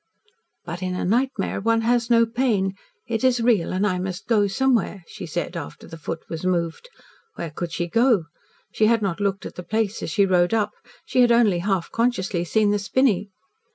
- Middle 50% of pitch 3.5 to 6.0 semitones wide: Yes, average, 4.3 semitones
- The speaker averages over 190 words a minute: Yes, average, 200 wpm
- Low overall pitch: No, high, 205 Hz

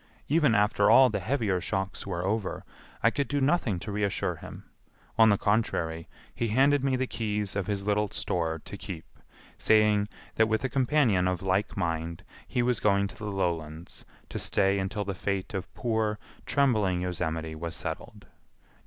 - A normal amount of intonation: Yes, average, 3.7 semitones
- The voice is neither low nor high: No, low, 105 Hz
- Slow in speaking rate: No, average, 170 wpm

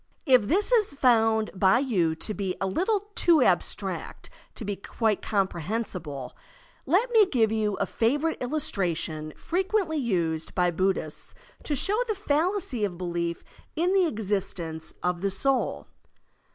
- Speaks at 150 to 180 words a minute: No, average, 140 wpm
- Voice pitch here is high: Yes, high, 220 Hz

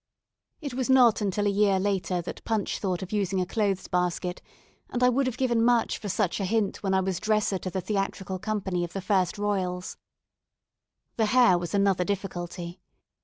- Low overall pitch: No, high, 195 Hz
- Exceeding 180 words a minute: Yes, average, 190 wpm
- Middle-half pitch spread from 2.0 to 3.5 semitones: Yes, average, 2.8 semitones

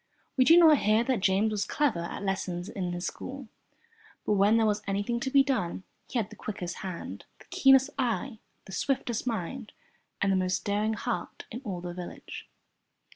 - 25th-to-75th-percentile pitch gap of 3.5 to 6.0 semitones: Yes, average, 5.1 semitones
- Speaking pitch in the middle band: No, high, 210 Hz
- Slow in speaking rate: No, average, 185 wpm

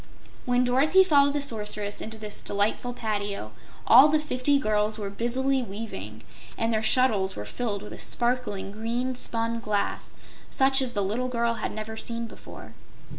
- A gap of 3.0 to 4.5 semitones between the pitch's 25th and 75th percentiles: Yes, average, 3.3 semitones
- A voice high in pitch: Yes, high, 230 Hz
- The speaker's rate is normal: Yes, average, 165 wpm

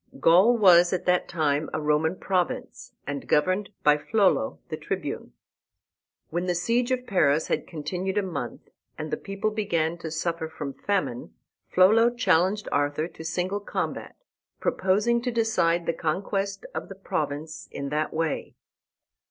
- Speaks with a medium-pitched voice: Yes, medium, 175 Hz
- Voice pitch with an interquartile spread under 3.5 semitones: No, average, 4.2 semitones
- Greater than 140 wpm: Yes, average, 150 wpm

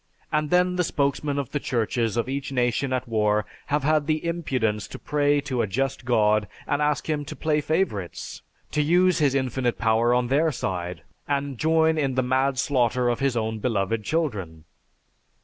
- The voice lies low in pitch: Yes, low, 130 Hz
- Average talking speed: Yes, average, 185 wpm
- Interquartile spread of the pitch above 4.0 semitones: Yes, average, 4.6 semitones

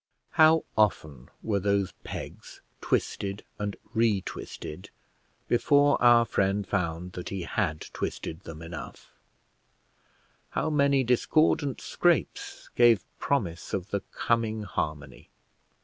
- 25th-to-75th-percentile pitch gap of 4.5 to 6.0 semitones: Yes, average, 5.2 semitones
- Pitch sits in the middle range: No, low, 100 Hz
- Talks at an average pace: No, slow, 110 wpm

